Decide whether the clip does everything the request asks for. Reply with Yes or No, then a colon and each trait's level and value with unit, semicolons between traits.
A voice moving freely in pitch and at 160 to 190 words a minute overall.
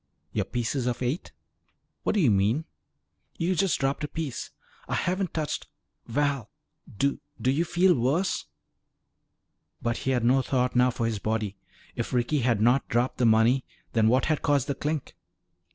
No: average, 4.0 semitones; average, 170 wpm